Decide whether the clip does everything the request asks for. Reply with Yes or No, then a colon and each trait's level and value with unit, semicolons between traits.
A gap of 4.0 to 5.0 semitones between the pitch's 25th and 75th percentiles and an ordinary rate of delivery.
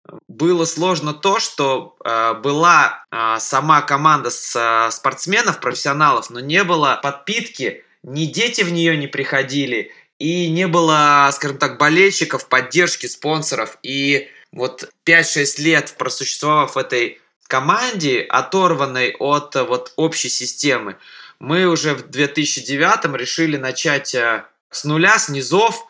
No: average, 3.6 semitones; average, 125 wpm